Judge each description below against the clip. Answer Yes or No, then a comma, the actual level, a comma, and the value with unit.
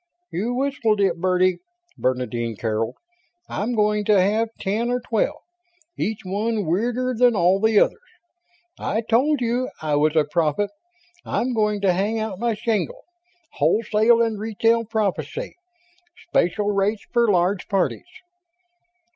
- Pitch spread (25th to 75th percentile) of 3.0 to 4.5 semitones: Yes, average, 3.8 semitones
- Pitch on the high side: Yes, high, 210 Hz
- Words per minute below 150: Yes, slow, 135 wpm